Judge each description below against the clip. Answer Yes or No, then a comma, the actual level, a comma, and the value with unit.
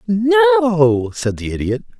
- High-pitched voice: Yes, high, 195 Hz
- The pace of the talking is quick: No, slow, 120 wpm